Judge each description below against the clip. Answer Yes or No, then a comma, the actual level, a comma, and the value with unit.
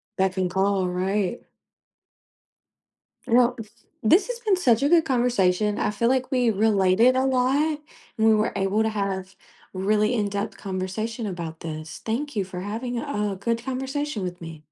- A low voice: No, high, 215 Hz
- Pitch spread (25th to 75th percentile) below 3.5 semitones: No, average, 4.5 semitones